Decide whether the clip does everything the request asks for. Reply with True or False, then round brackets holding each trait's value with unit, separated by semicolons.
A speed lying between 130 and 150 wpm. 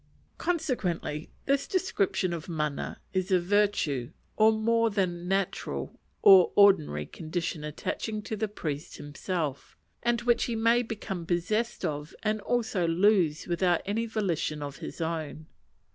True (135 wpm)